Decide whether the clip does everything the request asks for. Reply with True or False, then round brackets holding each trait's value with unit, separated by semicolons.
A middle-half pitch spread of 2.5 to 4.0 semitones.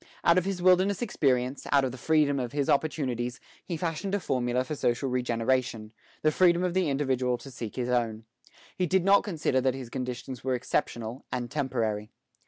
False (4.7 semitones)